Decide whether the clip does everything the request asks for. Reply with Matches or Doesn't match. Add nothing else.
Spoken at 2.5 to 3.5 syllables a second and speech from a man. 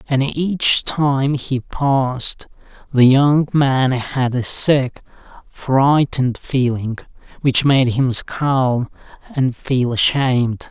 Matches